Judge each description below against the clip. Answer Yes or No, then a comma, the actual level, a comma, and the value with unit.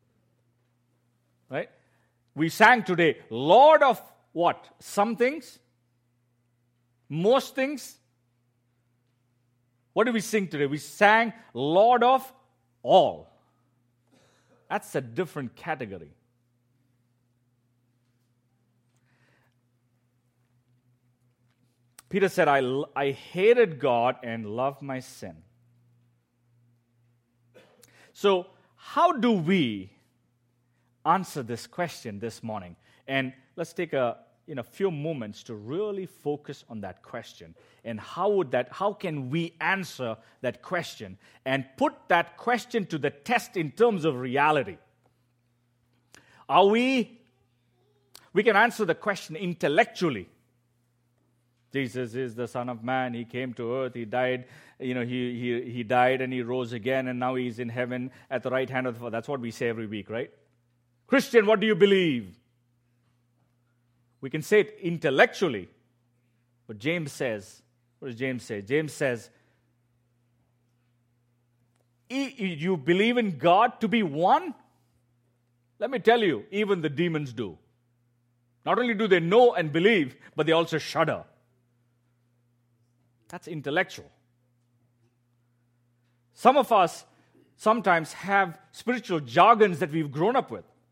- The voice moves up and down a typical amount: No, wide, 5.9 semitones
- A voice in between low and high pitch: No, low, 125 Hz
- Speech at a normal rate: No, slow, 125 wpm